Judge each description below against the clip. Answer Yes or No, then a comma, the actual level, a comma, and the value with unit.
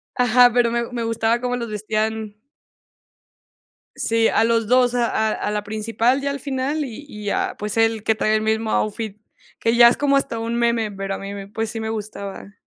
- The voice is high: Yes, high, 225 Hz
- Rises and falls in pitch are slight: Yes, narrow, 2.0 semitones